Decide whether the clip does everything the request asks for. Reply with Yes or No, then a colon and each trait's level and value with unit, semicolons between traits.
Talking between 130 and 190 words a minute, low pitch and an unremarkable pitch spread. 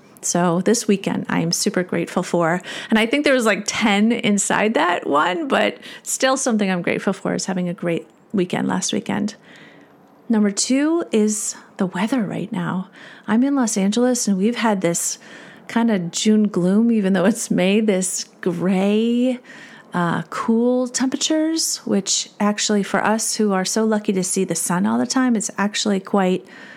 No: average, 175 wpm; high, 215 Hz; average, 3.8 semitones